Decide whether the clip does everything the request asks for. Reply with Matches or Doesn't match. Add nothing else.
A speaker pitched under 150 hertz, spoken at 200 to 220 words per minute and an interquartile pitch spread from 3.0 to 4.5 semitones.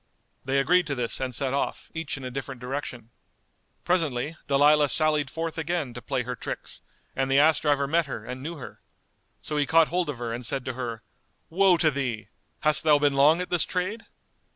Matches